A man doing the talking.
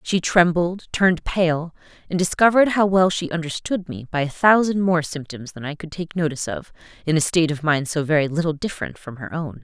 No: female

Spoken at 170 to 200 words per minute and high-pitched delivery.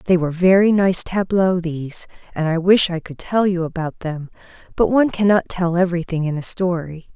No: average, 195 wpm; medium, 175 Hz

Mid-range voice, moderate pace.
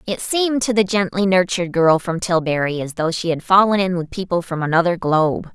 No: medium, 180 Hz; fast, 215 wpm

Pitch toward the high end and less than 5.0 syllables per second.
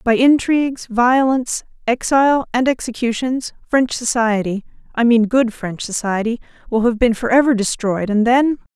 Yes: high, 240 Hz; 4.8 syllables/s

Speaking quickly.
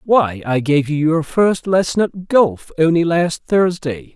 No: average, 175 wpm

